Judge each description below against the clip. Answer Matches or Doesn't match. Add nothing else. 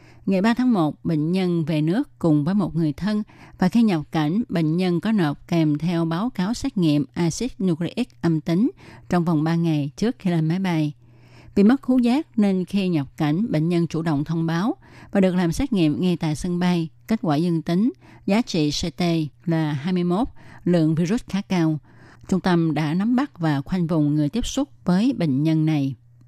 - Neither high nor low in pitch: Matches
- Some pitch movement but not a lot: Matches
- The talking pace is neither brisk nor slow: Matches